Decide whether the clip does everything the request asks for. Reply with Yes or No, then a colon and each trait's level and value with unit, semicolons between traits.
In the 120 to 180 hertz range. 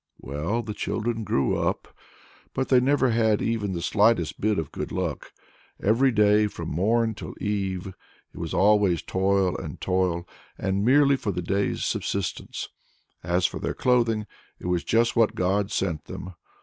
No: low, 100 Hz